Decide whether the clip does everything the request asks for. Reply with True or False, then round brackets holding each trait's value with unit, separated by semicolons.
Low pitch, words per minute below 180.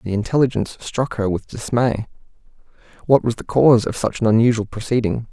True (115 Hz; 170 wpm)